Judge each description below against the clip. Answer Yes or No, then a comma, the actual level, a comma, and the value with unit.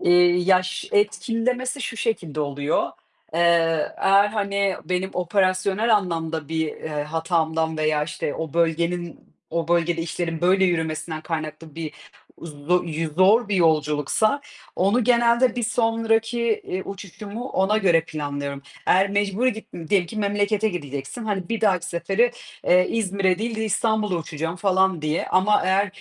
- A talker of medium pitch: Yes, medium, 180 Hz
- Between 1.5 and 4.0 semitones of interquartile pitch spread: No, average, 4.4 semitones